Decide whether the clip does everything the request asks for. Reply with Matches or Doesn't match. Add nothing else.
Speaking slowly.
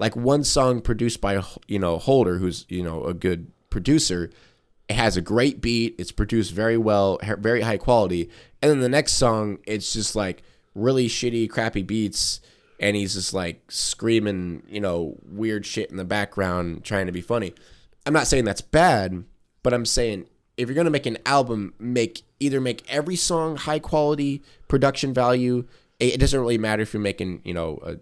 Doesn't match